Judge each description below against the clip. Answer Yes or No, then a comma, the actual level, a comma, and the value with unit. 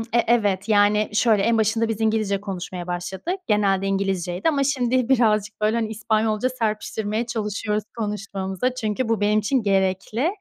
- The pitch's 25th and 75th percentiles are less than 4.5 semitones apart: Yes, narrow, 2.5 semitones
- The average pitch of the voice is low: No, high, 215 Hz